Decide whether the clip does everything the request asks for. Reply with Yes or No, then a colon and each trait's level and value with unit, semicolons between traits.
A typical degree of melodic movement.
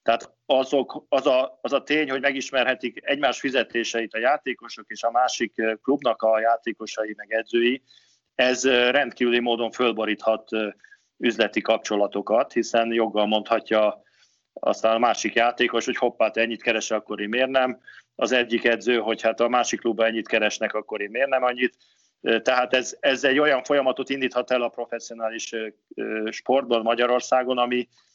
No: narrow, 2.3 semitones